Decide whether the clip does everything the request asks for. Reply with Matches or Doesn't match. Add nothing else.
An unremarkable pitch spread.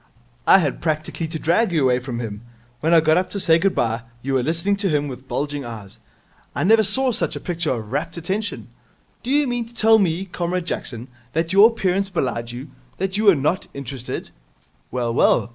Doesn't match